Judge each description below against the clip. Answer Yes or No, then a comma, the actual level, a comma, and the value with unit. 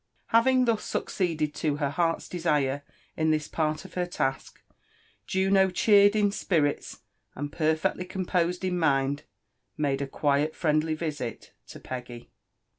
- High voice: No, medium, 160 Hz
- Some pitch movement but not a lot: Yes, average, 4.1 semitones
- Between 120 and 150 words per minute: Yes, slow, 135 wpm